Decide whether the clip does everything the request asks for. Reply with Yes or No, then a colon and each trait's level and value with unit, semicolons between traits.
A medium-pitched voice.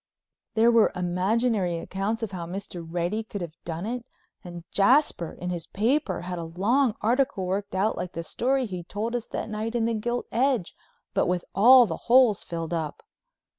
No: high, 205 Hz